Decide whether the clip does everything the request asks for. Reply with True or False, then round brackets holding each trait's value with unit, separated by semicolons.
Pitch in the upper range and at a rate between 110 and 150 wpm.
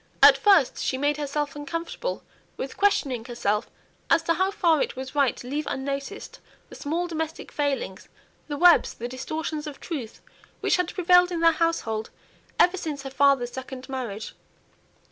False (290 Hz; 165 wpm)